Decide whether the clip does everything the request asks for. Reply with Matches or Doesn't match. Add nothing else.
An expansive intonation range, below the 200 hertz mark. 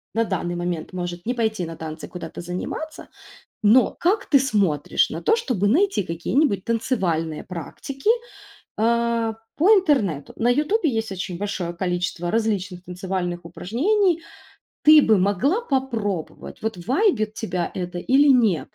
Doesn't match